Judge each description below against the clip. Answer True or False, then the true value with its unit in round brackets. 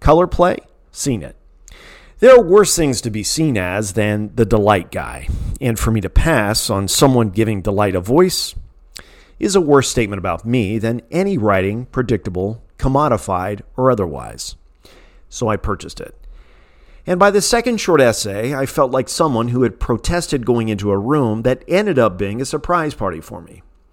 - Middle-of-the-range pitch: False (115 Hz)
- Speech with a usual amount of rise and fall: False (6.7 semitones)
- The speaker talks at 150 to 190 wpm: True (175 wpm)